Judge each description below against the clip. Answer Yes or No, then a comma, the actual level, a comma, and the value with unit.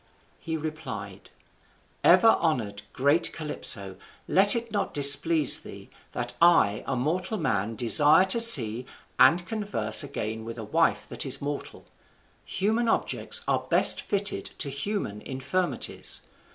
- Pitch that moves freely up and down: Yes, wide, 7.8 semitones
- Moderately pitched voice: Yes, medium, 150 Hz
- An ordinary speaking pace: No, slow, 130 wpm